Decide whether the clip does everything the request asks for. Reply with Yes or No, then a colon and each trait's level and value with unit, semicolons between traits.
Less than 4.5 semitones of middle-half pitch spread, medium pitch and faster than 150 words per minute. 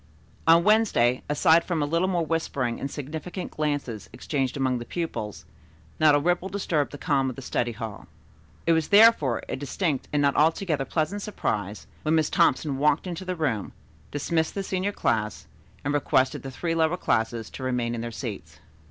No: average, 4.9 semitones; medium, 145 Hz; average, 180 wpm